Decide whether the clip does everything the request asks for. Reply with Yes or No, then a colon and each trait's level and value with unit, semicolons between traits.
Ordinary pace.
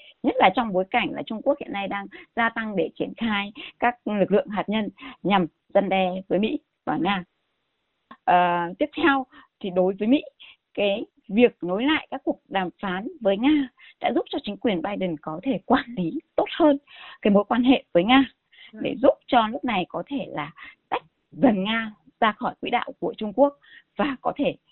Yes: average, 205 wpm